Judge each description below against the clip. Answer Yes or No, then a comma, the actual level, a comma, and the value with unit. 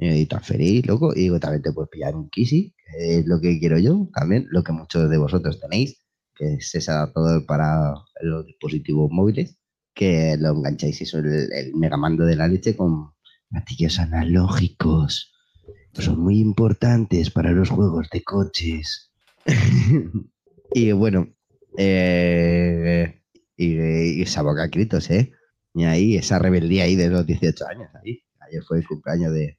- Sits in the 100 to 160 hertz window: No, very low, 85 Hz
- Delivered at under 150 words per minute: No, average, 160 wpm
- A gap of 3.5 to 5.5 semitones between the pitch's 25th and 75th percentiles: No, narrow, 2.5 semitones